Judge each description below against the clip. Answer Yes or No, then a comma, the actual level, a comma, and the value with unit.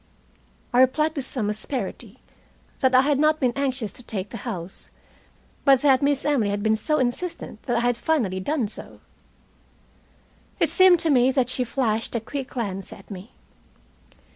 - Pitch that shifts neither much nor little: Yes, average, 4.3 semitones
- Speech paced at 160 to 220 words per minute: Yes, average, 170 wpm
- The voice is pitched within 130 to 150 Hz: No, very high, 255 Hz